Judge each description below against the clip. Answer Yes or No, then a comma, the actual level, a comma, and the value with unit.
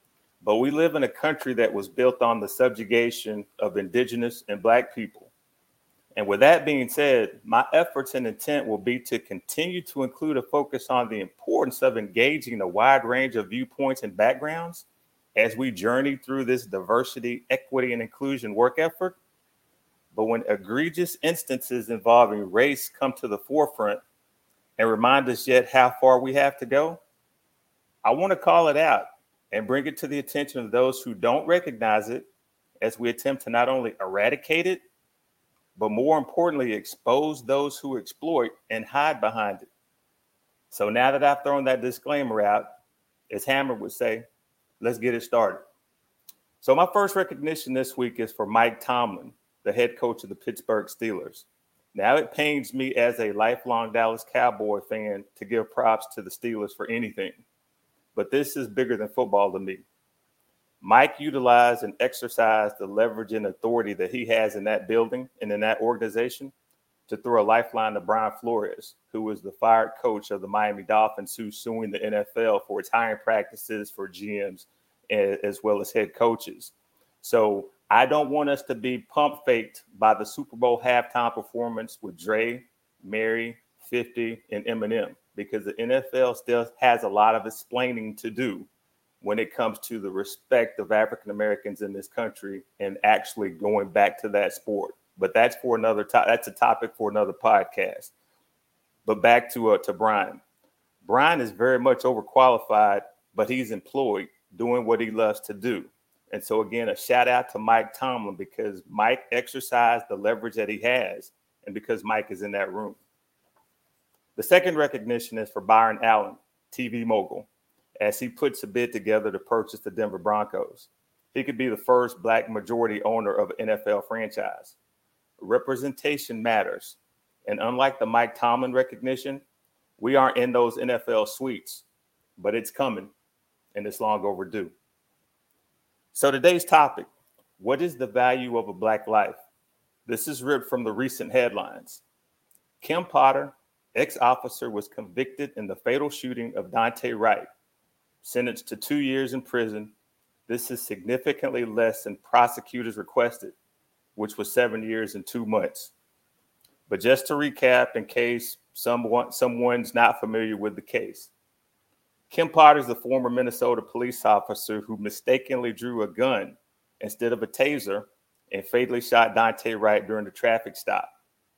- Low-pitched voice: Yes, low, 120 Hz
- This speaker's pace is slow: No, average, 165 wpm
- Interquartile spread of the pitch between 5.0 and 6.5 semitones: No, average, 3.4 semitones